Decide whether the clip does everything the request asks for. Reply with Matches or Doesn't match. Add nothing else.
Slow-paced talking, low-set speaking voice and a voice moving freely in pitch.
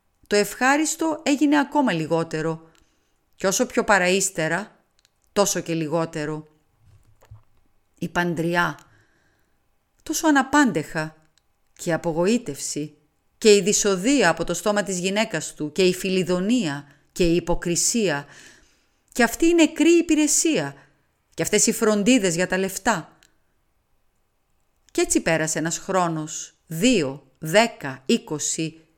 Doesn't match